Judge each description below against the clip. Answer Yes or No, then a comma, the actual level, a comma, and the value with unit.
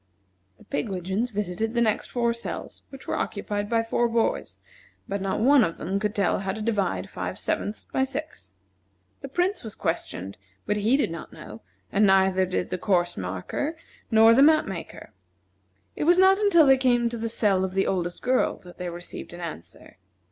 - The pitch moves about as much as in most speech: Yes, average, 4.9 semitones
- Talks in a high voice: Yes, high, 210 Hz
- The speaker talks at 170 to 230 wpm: Yes, average, 190 wpm